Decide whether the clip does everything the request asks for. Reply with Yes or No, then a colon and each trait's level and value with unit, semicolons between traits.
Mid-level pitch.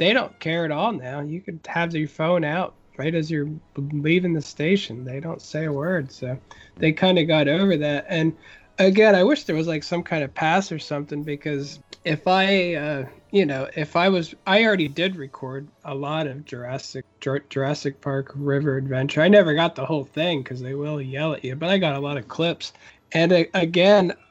Yes: medium, 155 Hz